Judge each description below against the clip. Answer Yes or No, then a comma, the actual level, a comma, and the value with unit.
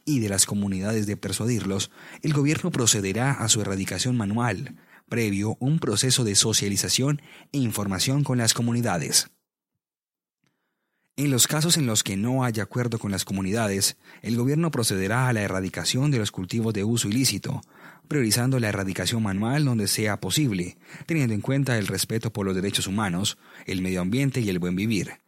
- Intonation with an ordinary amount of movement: Yes, average, 4.7 semitones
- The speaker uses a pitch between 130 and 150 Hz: No, low, 110 Hz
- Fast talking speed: No, average, 165 wpm